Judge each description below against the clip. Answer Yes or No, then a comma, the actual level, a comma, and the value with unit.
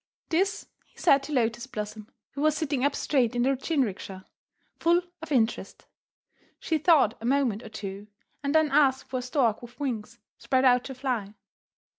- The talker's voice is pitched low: No, very high, 260 Hz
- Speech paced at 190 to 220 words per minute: No, average, 175 wpm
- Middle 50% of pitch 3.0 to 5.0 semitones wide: Yes, average, 4.1 semitones